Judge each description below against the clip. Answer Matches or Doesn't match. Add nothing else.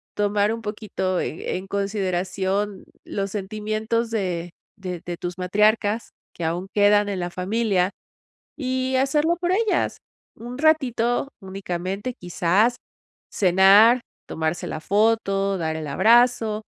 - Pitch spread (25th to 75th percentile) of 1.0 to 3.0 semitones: Doesn't match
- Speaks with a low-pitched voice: Doesn't match